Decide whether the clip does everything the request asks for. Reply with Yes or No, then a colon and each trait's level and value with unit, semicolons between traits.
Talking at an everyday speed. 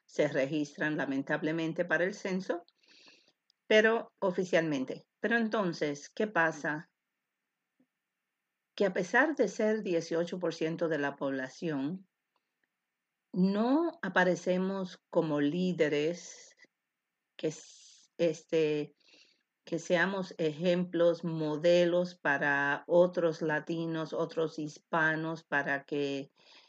No: slow, 85 wpm